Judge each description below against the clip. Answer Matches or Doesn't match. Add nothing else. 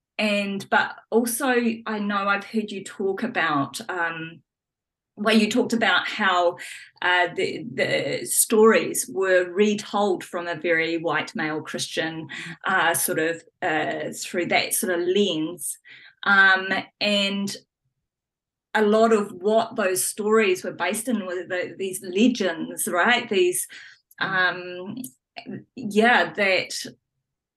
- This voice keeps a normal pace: Doesn't match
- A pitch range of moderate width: Matches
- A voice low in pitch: Doesn't match